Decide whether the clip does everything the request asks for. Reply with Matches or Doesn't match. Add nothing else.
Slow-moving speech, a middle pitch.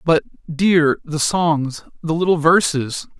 Matches